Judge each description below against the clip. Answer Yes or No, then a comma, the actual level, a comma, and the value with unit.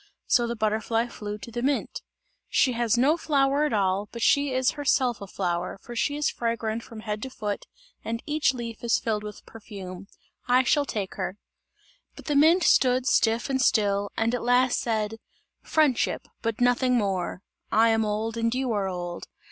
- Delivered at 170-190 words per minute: Yes, average, 185 wpm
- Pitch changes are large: No, average, 3.5 semitones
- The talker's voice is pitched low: No, high, 230 Hz